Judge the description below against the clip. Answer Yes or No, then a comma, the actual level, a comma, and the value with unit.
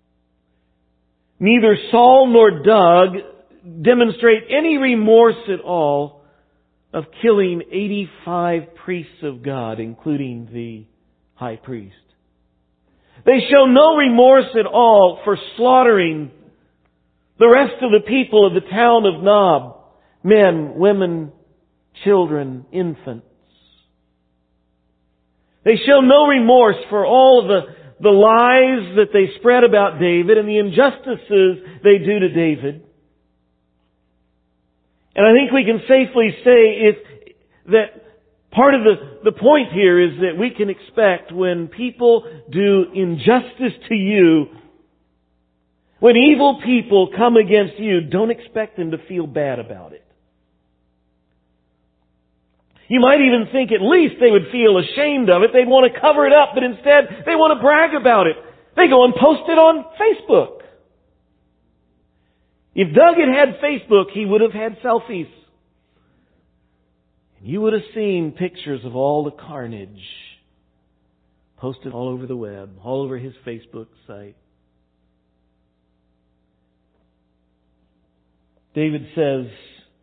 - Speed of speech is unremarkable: No, slow, 125 wpm